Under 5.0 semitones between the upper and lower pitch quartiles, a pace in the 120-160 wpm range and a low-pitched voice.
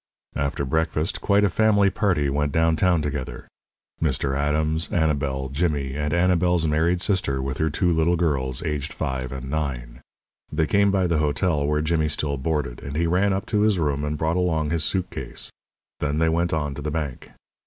No: average, 3.3 semitones; average, 185 wpm; very low, 75 Hz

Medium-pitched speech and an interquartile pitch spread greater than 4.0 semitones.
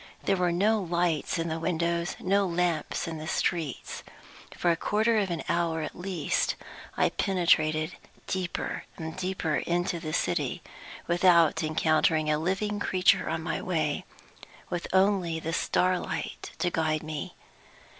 No: medium, 170 Hz; narrow, 2.5 semitones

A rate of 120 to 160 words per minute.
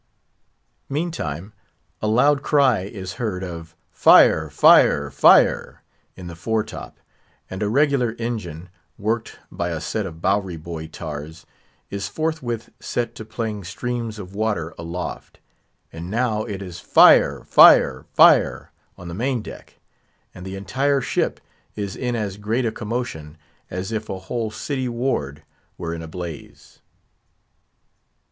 Yes: average, 140 wpm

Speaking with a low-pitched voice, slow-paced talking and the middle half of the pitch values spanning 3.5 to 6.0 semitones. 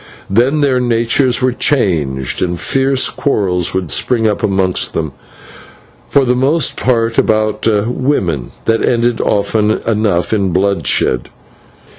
Yes: low, 110 Hz; slow, 125 wpm; average, 5.2 semitones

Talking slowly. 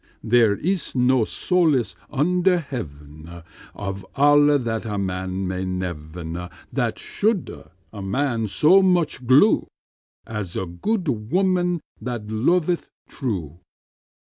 Yes: slow, 115 wpm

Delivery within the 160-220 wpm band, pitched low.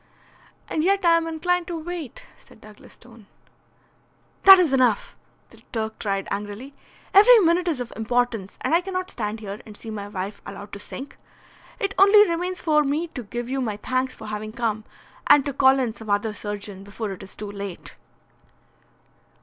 No: average, 180 wpm; high, 245 Hz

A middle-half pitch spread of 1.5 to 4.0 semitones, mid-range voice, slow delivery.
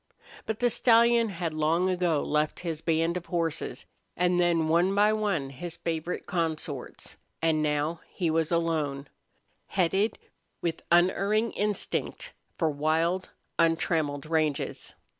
Yes: average, 2.8 semitones; medium, 165 Hz; slow, 125 wpm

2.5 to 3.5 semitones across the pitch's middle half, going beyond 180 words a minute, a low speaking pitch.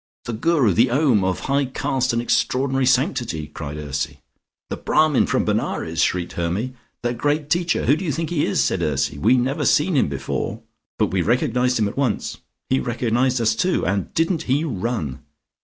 No: average, 5.2 semitones; average, 190 wpm; low, 125 Hz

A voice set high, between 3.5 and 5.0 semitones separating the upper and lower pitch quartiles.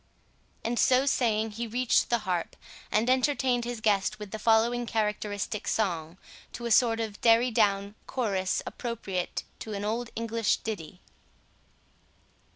No: high, 220 Hz; narrow, 2.6 semitones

